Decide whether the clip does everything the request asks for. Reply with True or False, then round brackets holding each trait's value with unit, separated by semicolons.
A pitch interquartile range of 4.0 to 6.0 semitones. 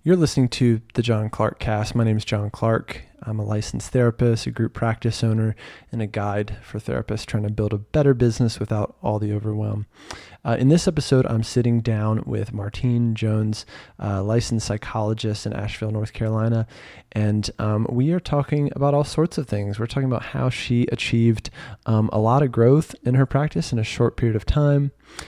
False (2.9 semitones)